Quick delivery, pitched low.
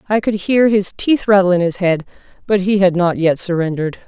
No: fast, 220 wpm; high, 190 Hz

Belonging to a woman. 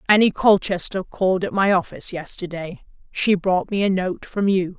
Yes: female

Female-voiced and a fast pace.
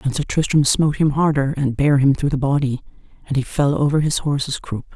Yes: female; fast, 230 wpm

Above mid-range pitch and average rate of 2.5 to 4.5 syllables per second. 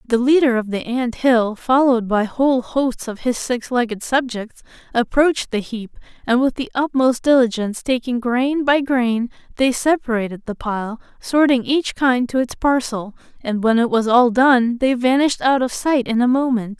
No: high, 245 Hz; 4.8 syllables/s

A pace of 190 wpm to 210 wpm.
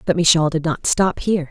No: fast, 240 wpm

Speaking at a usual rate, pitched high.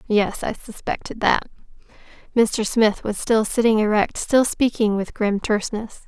Yes: average, 150 wpm; high, 215 Hz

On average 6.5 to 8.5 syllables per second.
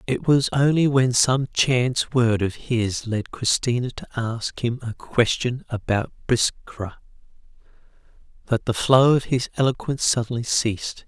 No: 4.3 syllables/s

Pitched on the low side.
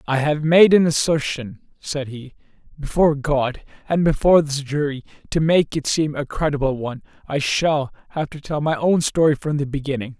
No: medium, 145 Hz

